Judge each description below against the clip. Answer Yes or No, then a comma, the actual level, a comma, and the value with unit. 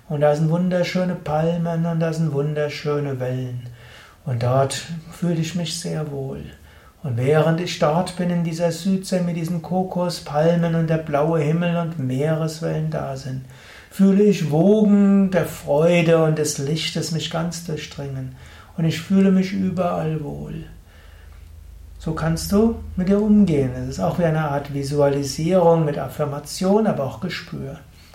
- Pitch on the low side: No, medium, 160 Hz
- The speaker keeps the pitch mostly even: No, average, 3.6 semitones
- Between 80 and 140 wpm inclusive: No, average, 150 wpm